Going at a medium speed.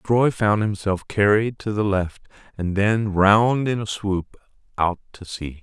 Yes: average, 170 wpm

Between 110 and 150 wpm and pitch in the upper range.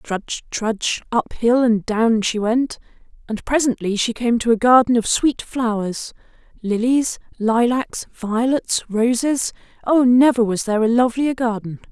Yes: average, 140 wpm; high, 235 Hz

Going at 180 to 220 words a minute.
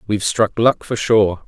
Yes: fast, 205 wpm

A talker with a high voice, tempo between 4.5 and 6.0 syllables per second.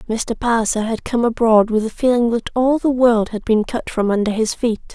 Yes: high, 230 Hz; 5.2 syllables/s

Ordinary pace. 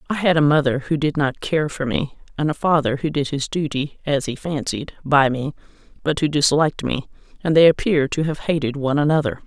No: fast, 215 wpm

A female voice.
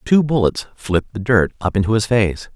No: male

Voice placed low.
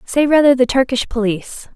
No: very high, 255 Hz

